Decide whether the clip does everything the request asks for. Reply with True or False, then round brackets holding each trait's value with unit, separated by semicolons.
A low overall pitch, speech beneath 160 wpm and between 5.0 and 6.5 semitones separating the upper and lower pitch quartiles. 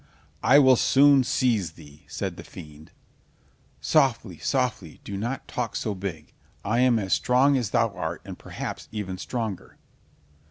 True (110 Hz; 150 wpm; 5.5 semitones)